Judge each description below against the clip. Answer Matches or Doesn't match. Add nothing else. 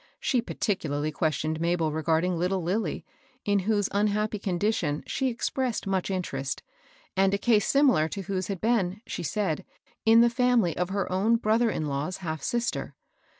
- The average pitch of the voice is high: Matches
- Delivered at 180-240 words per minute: Doesn't match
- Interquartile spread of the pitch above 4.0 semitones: Matches